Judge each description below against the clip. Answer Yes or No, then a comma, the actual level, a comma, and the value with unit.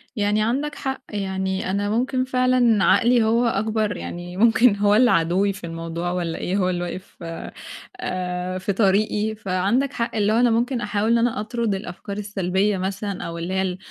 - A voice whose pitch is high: Yes, high, 205 Hz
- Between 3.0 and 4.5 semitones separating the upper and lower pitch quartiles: Yes, average, 3.7 semitones